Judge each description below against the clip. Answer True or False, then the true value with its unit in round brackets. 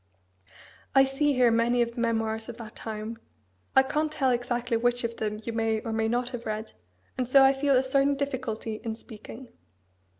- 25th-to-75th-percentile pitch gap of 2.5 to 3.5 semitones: True (2.9 semitones)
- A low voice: False (240 Hz)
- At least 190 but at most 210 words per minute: True (195 wpm)